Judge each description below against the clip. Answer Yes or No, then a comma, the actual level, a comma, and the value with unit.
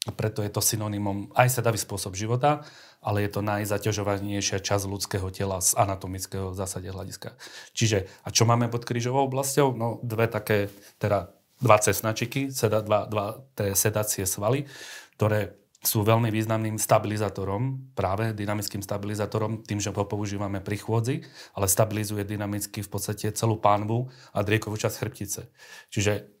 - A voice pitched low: Yes, low, 105 Hz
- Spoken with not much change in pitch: Yes, narrow, 2.1 semitones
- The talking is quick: No, average, 145 wpm